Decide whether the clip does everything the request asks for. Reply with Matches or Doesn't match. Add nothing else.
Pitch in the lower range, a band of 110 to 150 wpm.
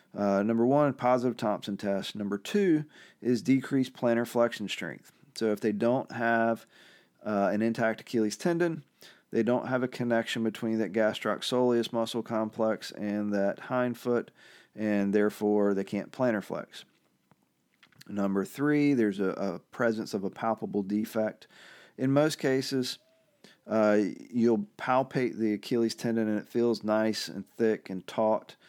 Matches